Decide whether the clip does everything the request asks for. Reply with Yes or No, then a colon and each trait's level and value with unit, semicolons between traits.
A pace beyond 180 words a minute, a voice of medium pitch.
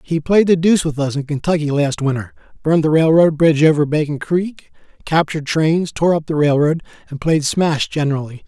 Yes: average, 190 wpm; medium, 155 Hz